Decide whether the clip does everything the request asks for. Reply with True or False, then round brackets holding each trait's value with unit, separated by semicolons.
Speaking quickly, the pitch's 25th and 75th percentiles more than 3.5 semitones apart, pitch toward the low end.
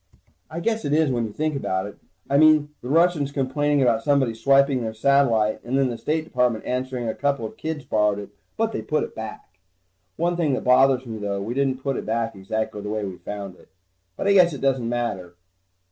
True (220 wpm; 4.7 semitones; 130 Hz)